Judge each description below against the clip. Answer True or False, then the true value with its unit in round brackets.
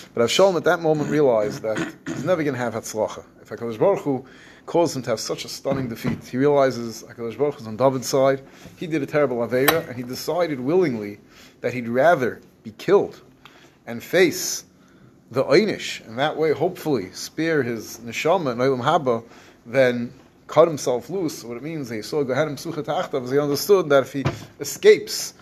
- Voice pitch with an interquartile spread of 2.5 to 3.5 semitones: False (4.1 semitones)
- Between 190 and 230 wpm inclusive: False (170 wpm)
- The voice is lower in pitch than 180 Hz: True (135 Hz)